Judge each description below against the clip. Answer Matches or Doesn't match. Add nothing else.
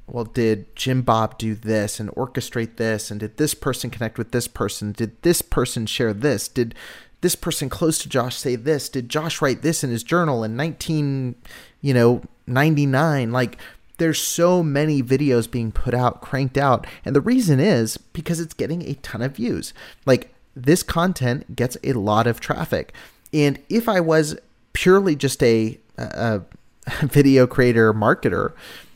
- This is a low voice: Matches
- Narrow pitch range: Doesn't match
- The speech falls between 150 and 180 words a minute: Matches